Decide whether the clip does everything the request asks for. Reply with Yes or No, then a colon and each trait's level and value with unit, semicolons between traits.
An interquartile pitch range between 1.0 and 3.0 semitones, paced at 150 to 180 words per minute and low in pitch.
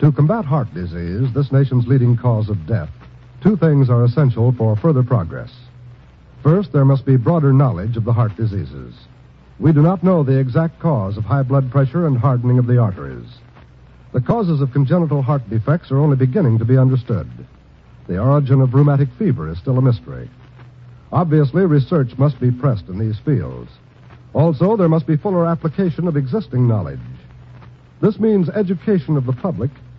No: average, 3.9 semitones; average, 175 wpm; low, 130 Hz